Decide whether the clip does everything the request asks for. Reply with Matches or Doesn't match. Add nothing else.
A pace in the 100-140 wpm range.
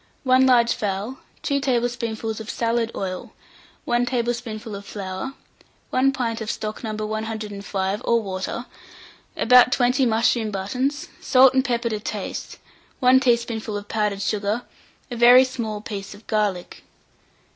Matches